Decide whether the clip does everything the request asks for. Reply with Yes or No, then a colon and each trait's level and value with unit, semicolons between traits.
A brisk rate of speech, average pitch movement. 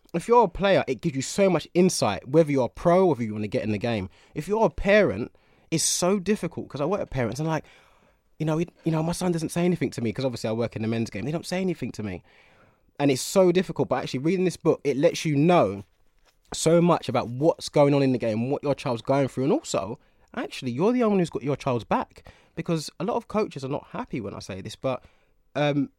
No: fast, 270 wpm; wide, 5.9 semitones